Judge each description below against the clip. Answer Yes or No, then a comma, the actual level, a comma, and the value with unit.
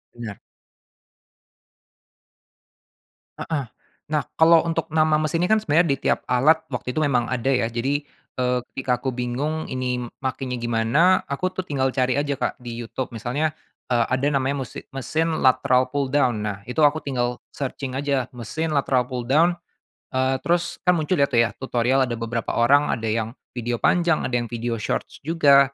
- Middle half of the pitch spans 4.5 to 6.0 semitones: No, average, 3.8 semitones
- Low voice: Yes, low, 130 Hz